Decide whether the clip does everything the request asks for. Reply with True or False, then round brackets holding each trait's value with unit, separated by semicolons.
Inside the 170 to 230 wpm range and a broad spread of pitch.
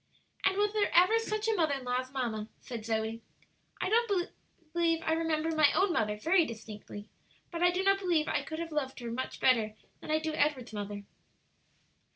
True (190 wpm; 7.4 semitones)